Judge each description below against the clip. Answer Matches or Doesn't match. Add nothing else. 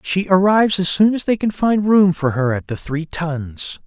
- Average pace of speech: Doesn't match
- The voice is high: Doesn't match